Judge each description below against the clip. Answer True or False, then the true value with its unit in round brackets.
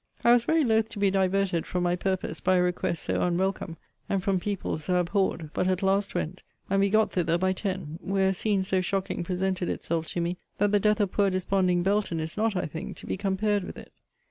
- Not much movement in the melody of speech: True (2.0 semitones)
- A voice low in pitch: False (190 Hz)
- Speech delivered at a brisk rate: True (230 wpm)